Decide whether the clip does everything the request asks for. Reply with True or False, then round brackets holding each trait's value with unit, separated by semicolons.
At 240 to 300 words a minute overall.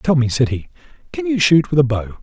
True (270 wpm)